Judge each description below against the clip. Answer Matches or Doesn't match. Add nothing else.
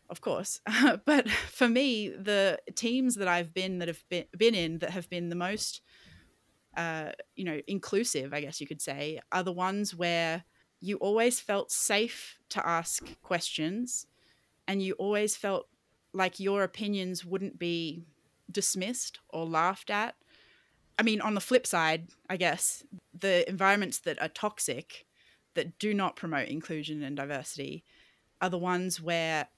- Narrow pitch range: Doesn't match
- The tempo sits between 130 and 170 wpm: Matches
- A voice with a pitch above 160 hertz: Matches